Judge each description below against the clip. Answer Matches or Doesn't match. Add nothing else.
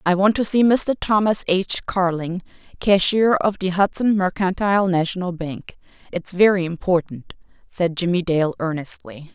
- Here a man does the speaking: Doesn't match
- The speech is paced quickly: Doesn't match